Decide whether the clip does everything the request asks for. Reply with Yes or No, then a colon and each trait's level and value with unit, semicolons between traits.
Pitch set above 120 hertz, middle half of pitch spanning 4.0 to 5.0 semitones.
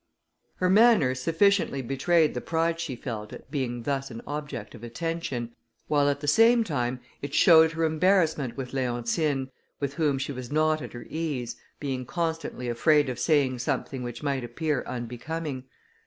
Yes: medium, 140 Hz; average, 4.4 semitones